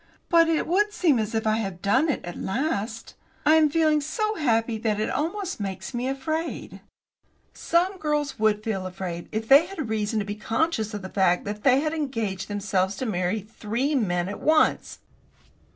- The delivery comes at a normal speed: Yes, average, 185 wpm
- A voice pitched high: Yes, high, 225 Hz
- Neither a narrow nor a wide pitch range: No, wide, 7.1 semitones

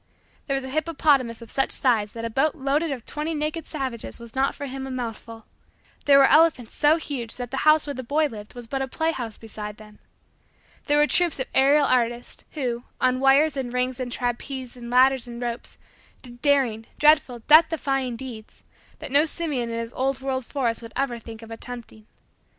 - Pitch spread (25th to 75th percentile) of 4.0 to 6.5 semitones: No, average, 3.4 semitones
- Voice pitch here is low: No, very high, 260 Hz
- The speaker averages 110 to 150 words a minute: No, average, 200 wpm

